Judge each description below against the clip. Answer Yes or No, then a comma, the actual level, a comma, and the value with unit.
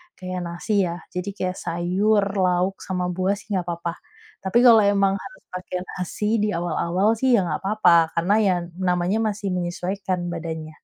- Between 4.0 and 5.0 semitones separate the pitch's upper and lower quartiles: No, narrow, 2.5 semitones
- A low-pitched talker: No, medium, 185 Hz